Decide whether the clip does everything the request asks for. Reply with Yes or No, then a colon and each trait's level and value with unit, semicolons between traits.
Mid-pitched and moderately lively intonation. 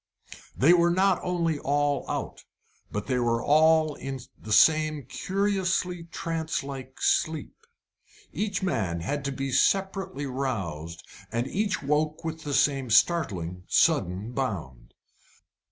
No: medium, 145 Hz; wide, 5.8 semitones